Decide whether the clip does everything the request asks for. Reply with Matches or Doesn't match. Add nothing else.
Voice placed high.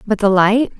Matches